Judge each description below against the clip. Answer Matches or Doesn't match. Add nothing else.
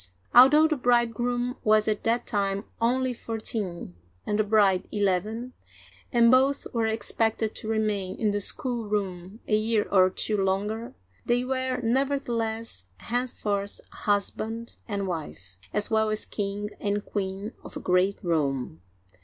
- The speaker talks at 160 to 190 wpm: Doesn't match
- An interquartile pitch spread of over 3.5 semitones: Doesn't match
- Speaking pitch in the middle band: Doesn't match